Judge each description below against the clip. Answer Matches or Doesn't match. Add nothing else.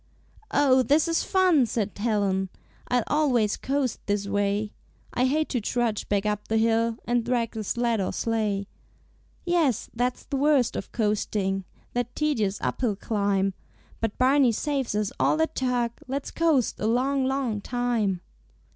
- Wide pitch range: Doesn't match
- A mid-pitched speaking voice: Doesn't match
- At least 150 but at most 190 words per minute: Matches